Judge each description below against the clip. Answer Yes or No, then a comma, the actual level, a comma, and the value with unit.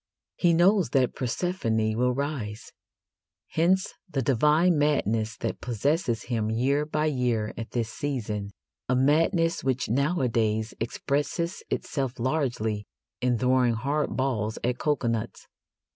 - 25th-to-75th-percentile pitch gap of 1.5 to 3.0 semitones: No, average, 4.8 semitones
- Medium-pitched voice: No, low, 130 Hz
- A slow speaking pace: Yes, slow, 120 wpm